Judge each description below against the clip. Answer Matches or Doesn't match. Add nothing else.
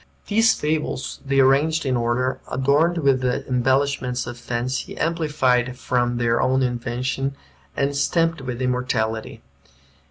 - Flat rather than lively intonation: Matches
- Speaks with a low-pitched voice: Matches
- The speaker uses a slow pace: Matches